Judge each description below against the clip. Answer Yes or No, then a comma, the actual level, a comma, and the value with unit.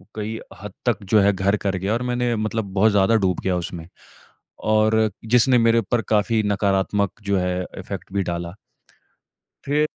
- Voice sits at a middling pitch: No, low, 105 Hz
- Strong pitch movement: No, average, 2.8 semitones